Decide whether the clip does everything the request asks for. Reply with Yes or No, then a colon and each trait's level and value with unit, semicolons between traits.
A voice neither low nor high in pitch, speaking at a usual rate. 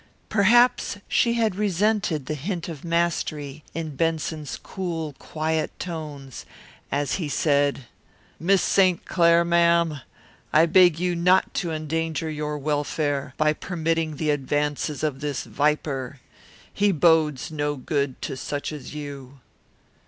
No: medium, 155 Hz; slow, 130 wpm